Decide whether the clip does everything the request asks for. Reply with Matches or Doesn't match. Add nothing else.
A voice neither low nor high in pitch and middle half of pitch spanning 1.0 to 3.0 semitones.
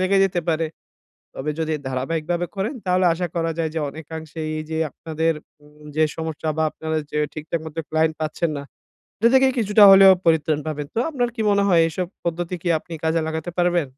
Matches